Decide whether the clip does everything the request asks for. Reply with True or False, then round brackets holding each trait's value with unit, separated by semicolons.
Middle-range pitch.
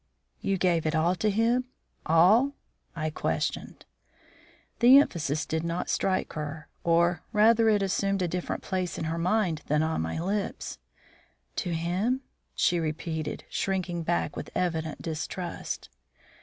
True (175 Hz)